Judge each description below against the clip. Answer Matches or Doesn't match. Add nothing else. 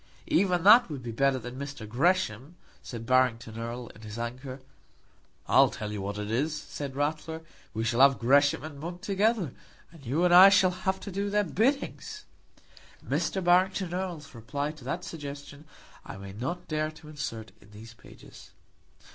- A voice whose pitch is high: Doesn't match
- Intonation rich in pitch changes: Matches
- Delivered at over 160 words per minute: Matches